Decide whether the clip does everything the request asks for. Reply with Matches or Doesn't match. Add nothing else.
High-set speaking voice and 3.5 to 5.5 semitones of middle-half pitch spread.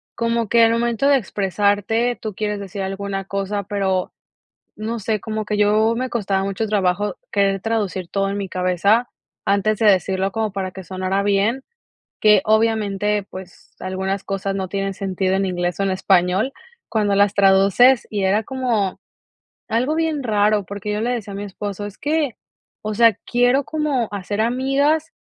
Doesn't match